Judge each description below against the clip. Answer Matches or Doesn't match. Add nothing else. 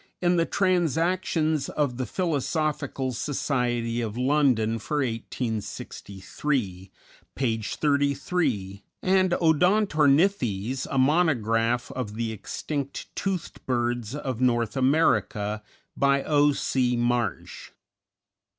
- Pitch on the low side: Matches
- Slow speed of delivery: Matches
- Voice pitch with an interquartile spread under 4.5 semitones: Doesn't match